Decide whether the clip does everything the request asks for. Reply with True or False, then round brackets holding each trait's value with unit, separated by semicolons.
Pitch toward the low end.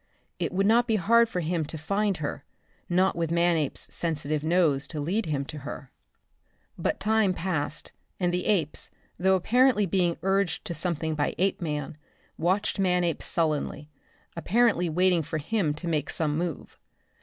False (175 Hz)